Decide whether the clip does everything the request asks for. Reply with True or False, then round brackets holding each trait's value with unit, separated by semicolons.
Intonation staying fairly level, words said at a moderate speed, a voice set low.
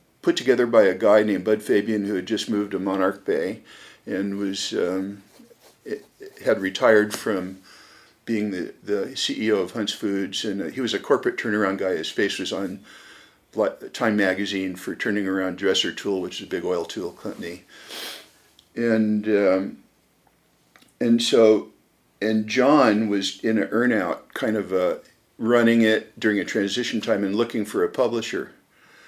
True (2.2 semitones; 160 wpm; 105 Hz)